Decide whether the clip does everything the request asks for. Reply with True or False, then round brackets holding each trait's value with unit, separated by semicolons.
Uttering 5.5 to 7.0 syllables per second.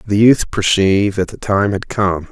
False (4.6 syllables/s)